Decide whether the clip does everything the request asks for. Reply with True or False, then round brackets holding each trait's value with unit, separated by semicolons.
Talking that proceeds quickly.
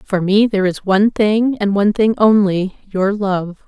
False (180 wpm)